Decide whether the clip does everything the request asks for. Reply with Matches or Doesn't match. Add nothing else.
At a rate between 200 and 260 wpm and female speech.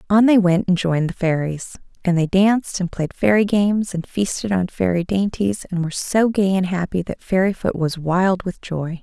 Matches